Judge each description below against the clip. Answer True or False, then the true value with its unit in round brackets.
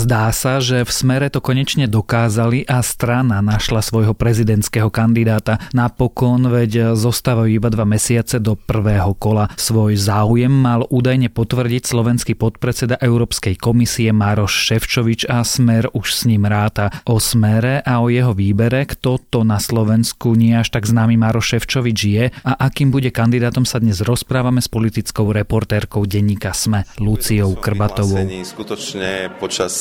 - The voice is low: True (115 Hz)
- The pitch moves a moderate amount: False (2.3 semitones)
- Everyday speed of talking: True (145 wpm)